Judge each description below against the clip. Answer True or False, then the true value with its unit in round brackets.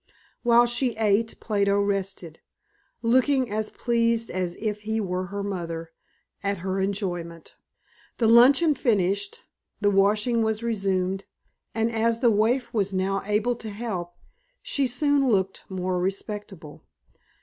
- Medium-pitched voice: False (210 Hz)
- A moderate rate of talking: False (130 wpm)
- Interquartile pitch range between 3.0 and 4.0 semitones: True (3.3 semitones)